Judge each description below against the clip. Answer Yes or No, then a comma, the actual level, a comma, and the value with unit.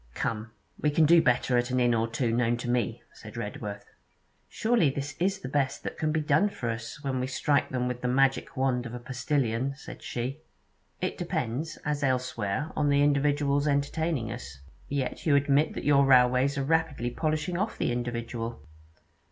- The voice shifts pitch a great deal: No, average, 3.3 semitones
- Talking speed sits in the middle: Yes, average, 185 wpm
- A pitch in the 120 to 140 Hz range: Yes, low, 135 Hz